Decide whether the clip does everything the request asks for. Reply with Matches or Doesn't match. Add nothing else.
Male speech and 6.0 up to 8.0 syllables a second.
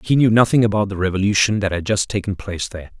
Matches